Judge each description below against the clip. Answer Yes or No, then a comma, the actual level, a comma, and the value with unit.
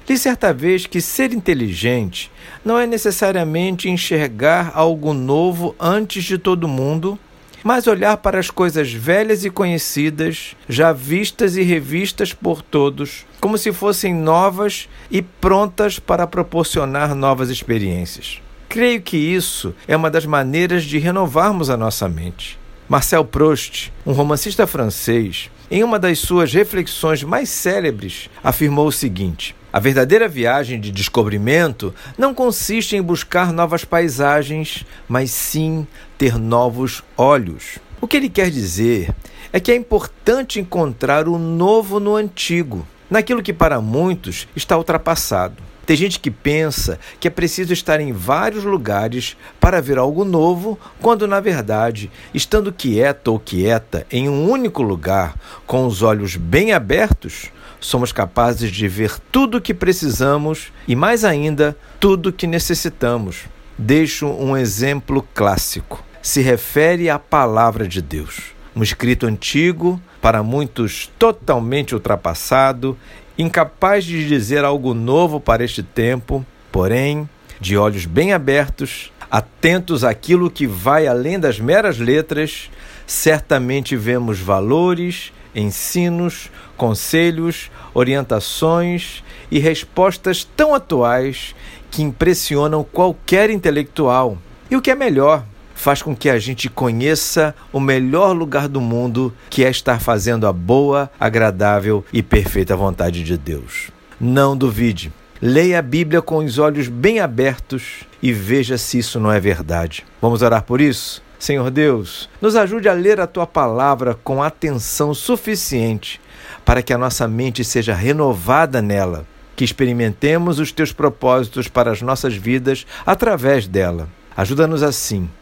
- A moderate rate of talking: Yes, average, 135 wpm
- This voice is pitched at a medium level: Yes, medium, 145 Hz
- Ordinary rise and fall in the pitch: No, wide, 6.7 semitones